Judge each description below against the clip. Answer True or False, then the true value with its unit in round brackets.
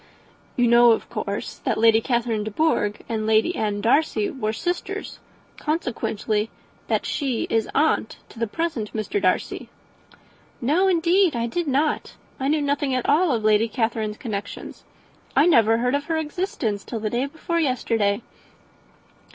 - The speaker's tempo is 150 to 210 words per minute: True (155 wpm)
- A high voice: True (240 Hz)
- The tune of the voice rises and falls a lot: True (5.8 semitones)